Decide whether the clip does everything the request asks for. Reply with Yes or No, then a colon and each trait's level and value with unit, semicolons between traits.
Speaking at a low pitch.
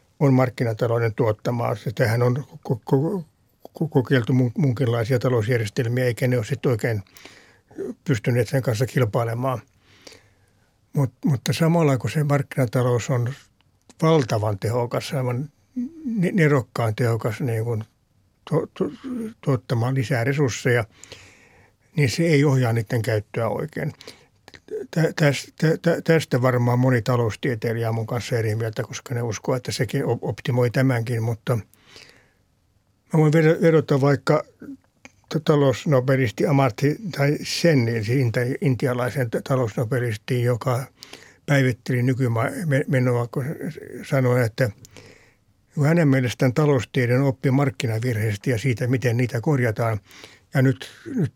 Yes: low, 130 Hz